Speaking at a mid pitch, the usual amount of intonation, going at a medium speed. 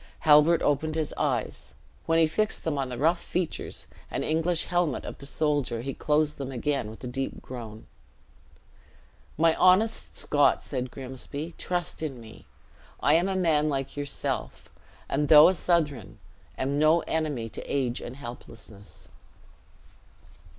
Yes: medium, 150 Hz; average, 3.7 semitones; average, 150 wpm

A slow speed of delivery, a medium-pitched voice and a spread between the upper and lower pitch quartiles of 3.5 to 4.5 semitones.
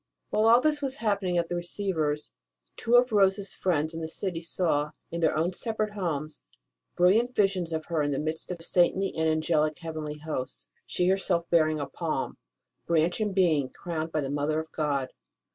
No: average, 195 wpm; medium, 170 Hz; average, 3.8 semitones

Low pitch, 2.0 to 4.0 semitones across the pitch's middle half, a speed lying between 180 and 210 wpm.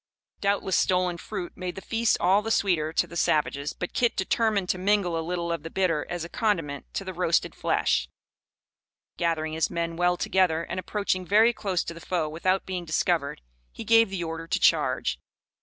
No: medium, 175 Hz; average, 2.8 semitones; average, 190 wpm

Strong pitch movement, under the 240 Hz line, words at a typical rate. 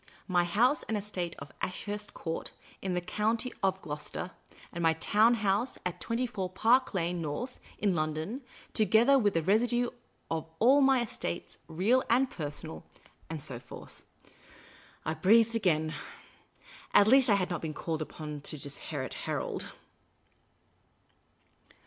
Yes: wide, 6.2 semitones; high, 190 Hz; average, 145 wpm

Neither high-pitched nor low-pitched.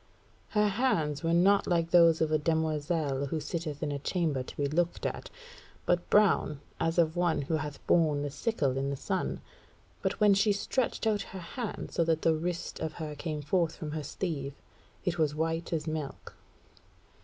Yes: medium, 160 Hz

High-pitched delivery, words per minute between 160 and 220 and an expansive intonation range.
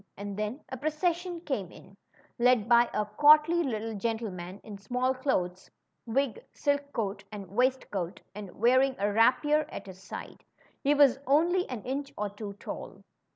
Yes: high, 240 Hz; average, 165 wpm; wide, 5.7 semitones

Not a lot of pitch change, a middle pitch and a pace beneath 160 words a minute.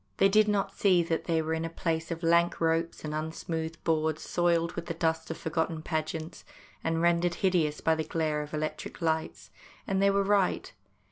No: narrow, 1.3 semitones; medium, 165 Hz; average, 195 wpm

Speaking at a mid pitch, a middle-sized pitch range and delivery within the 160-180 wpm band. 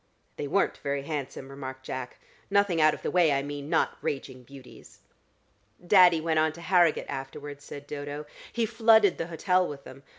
Yes: medium, 150 Hz; average, 4.1 semitones; average, 175 wpm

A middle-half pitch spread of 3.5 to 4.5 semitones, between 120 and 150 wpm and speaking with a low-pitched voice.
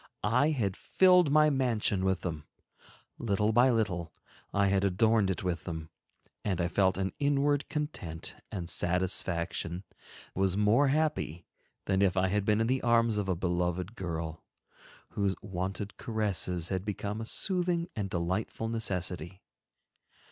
Yes: average, 4.2 semitones; average, 145 wpm; low, 100 Hz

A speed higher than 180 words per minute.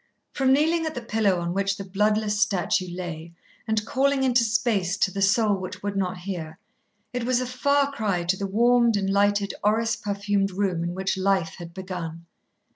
Yes: average, 190 wpm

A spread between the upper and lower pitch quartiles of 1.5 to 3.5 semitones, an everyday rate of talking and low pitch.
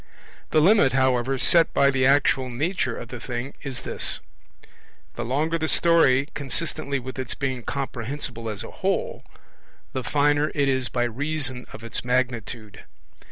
Yes: average, 2.9 semitones; average, 155 wpm; low, 130 Hz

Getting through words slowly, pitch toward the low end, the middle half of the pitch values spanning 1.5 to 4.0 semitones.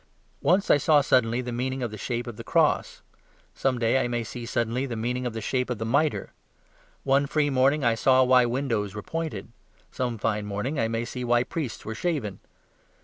No: fast, 205 wpm; low, 125 Hz; average, 2.8 semitones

